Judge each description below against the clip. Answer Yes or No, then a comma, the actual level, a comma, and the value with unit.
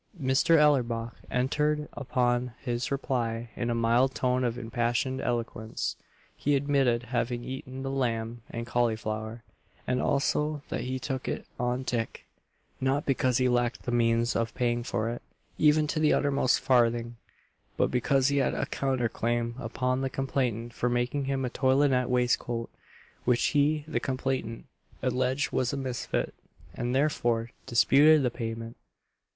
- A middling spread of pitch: No, narrow, 2.3 semitones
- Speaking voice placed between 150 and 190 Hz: No, low, 125 Hz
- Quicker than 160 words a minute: No, average, 150 wpm